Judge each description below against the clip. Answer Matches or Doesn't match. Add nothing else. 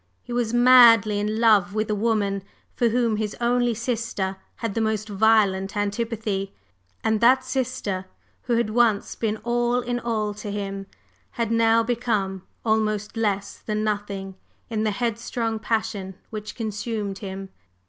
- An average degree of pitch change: Doesn't match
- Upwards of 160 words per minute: Doesn't match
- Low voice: Doesn't match